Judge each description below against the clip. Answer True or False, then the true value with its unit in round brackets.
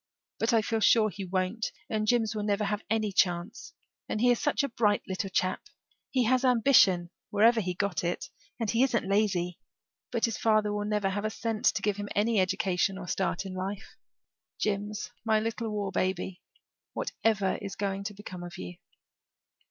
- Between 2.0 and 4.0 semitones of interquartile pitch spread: True (2.8 semitones)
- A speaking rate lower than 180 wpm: False (185 wpm)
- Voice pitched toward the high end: True (205 Hz)